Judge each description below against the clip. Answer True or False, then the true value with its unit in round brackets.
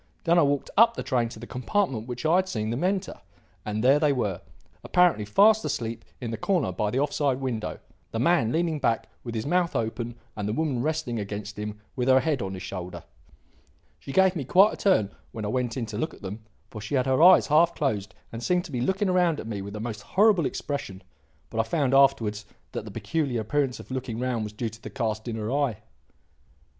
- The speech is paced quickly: True (230 wpm)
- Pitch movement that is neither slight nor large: False (6.3 semitones)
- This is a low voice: True (125 Hz)